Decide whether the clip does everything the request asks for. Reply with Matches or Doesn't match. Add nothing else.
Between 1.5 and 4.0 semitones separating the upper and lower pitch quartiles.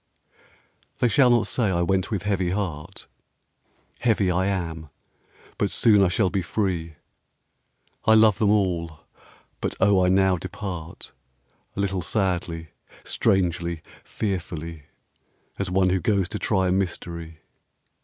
Matches